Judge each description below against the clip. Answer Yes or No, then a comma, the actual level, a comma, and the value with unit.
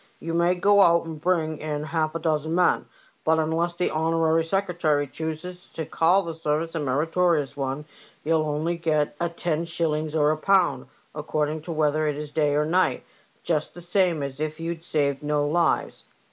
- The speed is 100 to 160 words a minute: No, average, 180 wpm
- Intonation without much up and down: Yes, narrow, 2.0 semitones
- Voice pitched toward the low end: No, medium, 160 Hz